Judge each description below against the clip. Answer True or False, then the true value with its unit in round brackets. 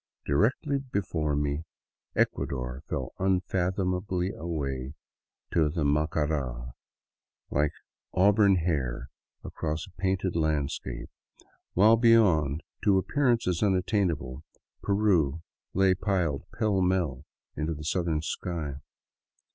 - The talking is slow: True (95 wpm)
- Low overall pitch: True (85 Hz)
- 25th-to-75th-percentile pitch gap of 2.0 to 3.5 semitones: False (4.7 semitones)